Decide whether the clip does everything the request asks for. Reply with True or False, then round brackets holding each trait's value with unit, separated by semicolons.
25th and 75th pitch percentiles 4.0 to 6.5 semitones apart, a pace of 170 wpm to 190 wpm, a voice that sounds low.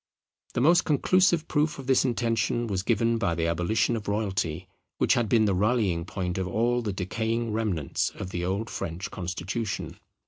True (4.3 semitones; 175 wpm; 110 Hz)